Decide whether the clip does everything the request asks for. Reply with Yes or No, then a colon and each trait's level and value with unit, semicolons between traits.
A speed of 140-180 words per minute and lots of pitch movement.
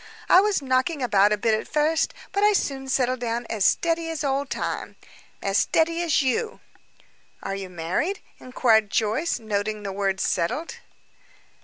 Yes: average, 160 wpm; wide, 7.7 semitones